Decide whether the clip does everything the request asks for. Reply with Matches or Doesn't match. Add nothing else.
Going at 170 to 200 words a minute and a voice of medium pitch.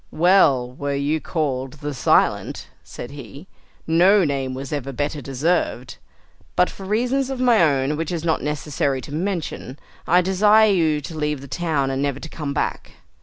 Matches